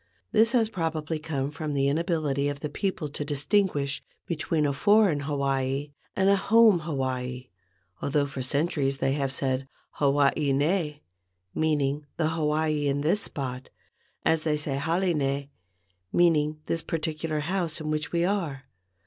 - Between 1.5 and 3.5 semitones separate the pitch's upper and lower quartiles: Yes, average, 2.9 semitones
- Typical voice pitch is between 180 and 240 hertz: No, medium, 150 Hz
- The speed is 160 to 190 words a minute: No, average, 150 wpm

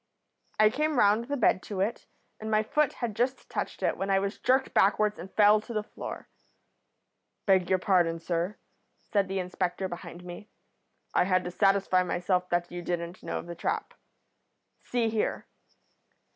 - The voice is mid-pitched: No, high, 195 Hz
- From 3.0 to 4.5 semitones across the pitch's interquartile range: Yes, average, 3.3 semitones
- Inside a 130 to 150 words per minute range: No, average, 170 wpm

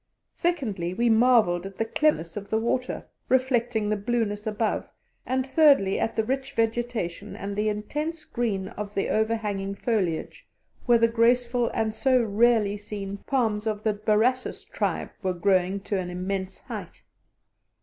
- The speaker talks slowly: No, average, 150 wpm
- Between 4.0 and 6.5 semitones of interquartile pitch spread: No, average, 3.3 semitones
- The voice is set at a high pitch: Yes, high, 220 Hz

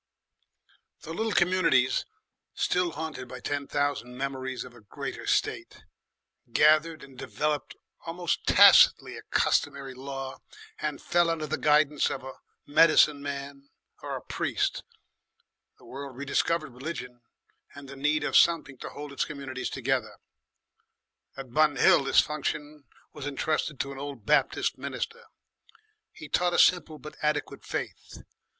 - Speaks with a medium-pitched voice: Yes, medium, 145 Hz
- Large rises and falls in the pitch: No, narrow, 2.4 semitones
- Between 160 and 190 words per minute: No, average, 140 wpm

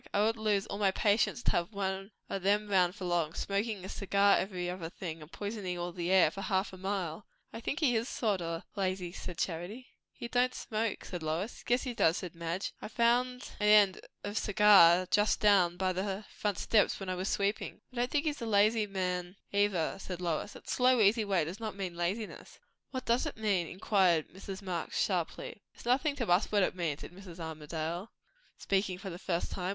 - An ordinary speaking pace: No, fast, 215 wpm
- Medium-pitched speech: No, high, 195 Hz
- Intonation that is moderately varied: Yes, average, 3.1 semitones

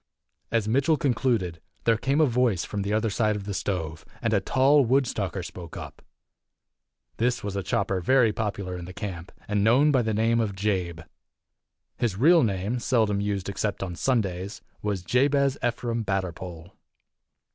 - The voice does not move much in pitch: No, average, 4.3 semitones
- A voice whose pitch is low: Yes, low, 105 Hz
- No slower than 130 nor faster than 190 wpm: Yes, average, 165 wpm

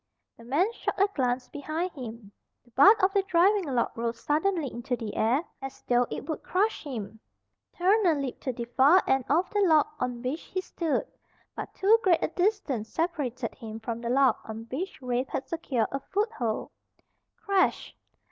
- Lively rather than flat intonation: Yes, wide, 7.2 semitones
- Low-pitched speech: No, very high, 275 Hz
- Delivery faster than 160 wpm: Yes, average, 180 wpm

